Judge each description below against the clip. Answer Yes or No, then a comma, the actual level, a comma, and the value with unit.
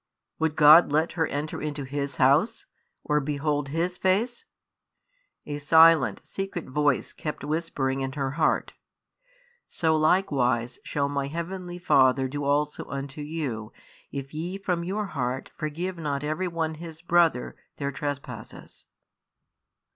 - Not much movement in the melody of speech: No, average, 3.1 semitones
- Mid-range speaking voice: Yes, medium, 150 Hz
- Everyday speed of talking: No, slow, 130 wpm